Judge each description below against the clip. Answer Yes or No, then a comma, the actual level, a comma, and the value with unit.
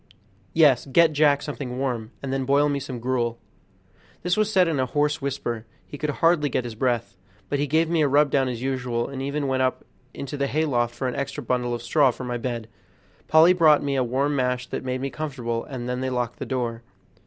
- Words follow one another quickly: Yes, fast, 225 wpm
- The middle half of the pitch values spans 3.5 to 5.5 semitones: No, average, 2.9 semitones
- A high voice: No, low, 135 Hz